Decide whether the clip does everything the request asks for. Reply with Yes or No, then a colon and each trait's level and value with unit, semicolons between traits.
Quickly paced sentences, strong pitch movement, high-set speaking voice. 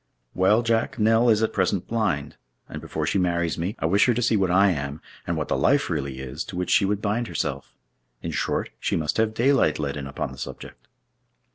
No: fast, 225 wpm; wide, 6.5 semitones; very low, 95 Hz